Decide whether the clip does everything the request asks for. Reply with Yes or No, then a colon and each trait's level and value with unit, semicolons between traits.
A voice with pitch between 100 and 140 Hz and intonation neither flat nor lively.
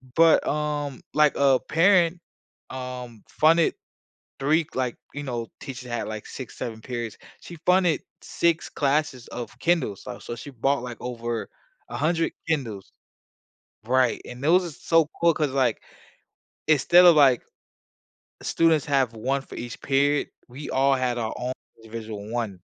Yes: low, 135 Hz; average, 4.4 semitones